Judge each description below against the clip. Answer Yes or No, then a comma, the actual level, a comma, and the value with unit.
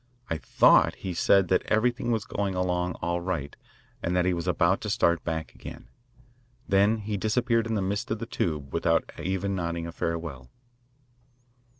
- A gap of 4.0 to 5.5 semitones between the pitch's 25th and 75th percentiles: No, average, 3.5 semitones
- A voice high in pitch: No, very low, 90 Hz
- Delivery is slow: No, average, 175 wpm